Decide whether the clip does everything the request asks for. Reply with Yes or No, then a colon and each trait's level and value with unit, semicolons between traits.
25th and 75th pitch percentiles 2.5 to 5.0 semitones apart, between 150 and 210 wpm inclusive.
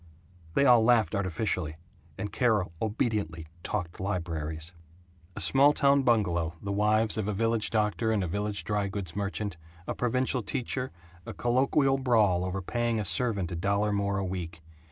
Yes: average, 4.1 semitones; average, 160 wpm